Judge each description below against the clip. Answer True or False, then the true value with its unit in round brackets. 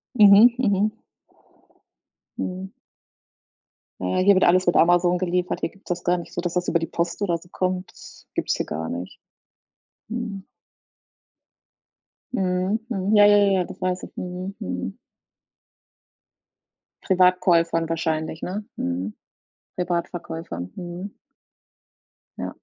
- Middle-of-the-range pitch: True (180 Hz)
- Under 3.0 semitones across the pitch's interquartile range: True (2.4 semitones)